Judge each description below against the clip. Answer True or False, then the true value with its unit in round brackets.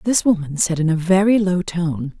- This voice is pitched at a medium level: True (175 Hz)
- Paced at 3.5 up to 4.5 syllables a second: False (4.9 syllables/s)